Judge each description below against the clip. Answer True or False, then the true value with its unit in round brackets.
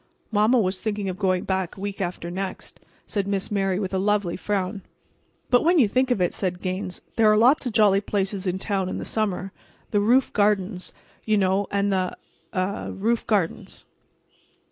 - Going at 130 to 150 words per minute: False (180 wpm)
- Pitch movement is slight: True (2.2 semitones)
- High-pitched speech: True (200 Hz)